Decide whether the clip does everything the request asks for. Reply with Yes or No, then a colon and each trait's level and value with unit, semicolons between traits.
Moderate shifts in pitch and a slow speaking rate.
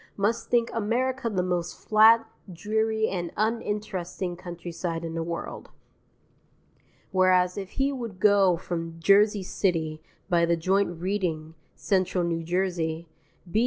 Yes: average, 3.8 semitones; slow, 125 wpm